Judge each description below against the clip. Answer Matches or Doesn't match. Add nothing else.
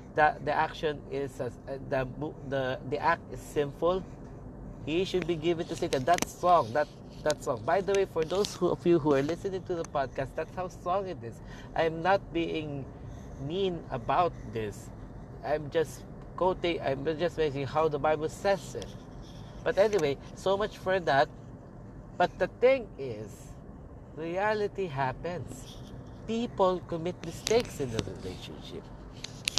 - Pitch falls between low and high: Matches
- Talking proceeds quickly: Doesn't match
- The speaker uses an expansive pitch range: Doesn't match